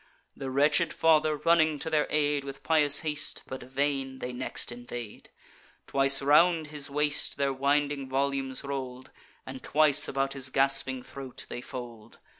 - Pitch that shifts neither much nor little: No, narrow, 2.1 semitones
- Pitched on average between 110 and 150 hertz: Yes, medium, 140 Hz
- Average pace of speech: Yes, average, 150 wpm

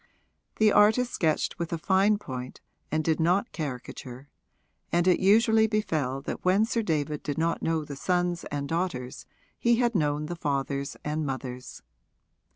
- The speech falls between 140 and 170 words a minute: Yes, average, 160 wpm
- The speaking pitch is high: No, medium, 165 Hz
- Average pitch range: No, wide, 5.7 semitones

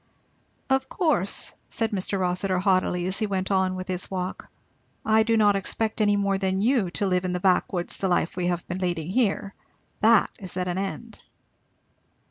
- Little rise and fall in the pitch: Yes, narrow, 2.3 semitones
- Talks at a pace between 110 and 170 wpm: No, average, 190 wpm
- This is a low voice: No, high, 190 Hz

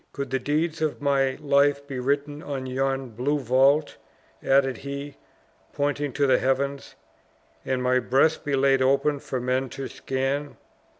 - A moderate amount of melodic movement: No, narrow, 1.5 semitones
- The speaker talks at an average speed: Yes, average, 155 wpm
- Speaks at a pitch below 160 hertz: Yes, medium, 140 Hz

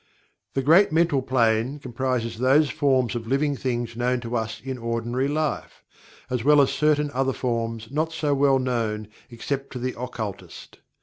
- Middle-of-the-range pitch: No, low, 130 Hz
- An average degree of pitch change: Yes, average, 3.3 semitones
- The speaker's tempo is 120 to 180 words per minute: Yes, average, 165 wpm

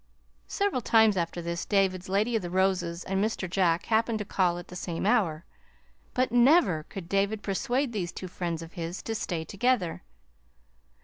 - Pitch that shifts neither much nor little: Yes, average, 4.1 semitones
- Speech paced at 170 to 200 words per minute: Yes, average, 175 wpm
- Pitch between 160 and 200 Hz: Yes, high, 190 Hz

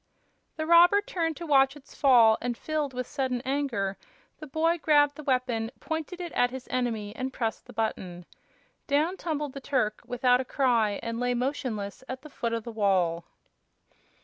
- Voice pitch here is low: No, very high, 255 Hz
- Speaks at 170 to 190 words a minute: Yes, average, 175 wpm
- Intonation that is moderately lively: Yes, average, 4.3 semitones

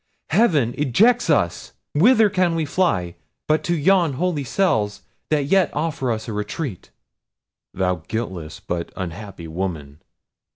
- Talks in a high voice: No, low, 135 Hz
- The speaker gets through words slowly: Yes, slow, 125 wpm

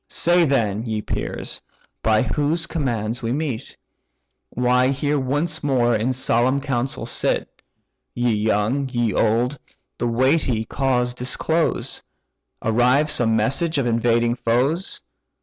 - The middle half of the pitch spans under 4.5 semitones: Yes, average, 3.3 semitones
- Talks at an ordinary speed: No, slow, 120 wpm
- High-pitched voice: No, low, 125 Hz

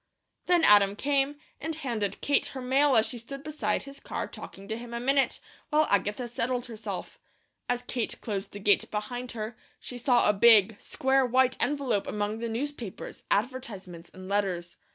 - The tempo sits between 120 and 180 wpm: Yes, average, 175 wpm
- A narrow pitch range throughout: No, average, 4.4 semitones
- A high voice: Yes, high, 235 Hz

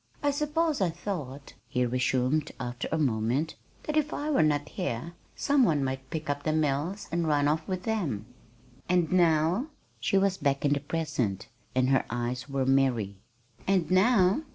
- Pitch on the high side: No, medium, 155 Hz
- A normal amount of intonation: No, wide, 5.8 semitones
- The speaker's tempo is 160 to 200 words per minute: Yes, average, 175 wpm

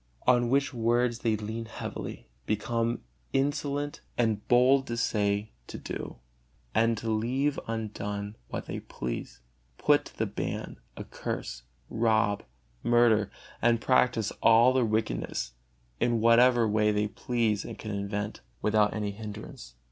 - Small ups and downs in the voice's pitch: Yes, narrow, 2.3 semitones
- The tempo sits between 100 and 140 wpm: Yes, slow, 135 wpm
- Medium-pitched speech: No, low, 115 Hz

